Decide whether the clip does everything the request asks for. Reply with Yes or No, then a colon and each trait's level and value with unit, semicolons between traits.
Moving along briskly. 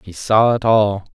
Yes: fast, 210 wpm